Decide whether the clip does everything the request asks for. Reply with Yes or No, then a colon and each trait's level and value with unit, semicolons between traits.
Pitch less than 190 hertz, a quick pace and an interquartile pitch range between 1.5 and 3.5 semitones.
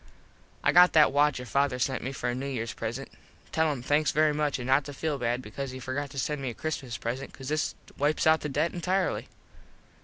Yes: medium, 140 Hz; fast, 235 wpm; average, 2.9 semitones